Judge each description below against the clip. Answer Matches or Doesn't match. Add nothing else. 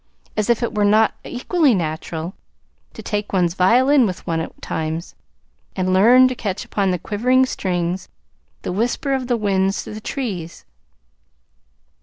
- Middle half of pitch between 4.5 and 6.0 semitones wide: Matches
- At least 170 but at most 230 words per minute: Doesn't match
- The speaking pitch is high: Matches